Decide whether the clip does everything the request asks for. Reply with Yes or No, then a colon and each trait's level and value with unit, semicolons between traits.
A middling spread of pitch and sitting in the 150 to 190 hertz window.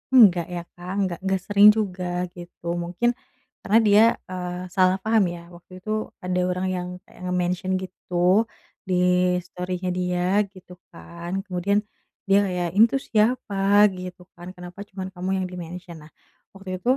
No: narrow, 1.6 semitones; medium, 185 Hz